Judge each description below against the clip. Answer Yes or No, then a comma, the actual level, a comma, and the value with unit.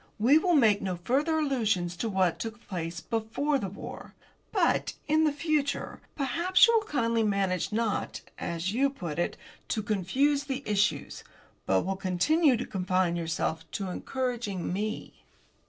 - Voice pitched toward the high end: Yes, high, 220 Hz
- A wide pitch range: Yes, wide, 7.1 semitones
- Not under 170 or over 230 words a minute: No, average, 155 wpm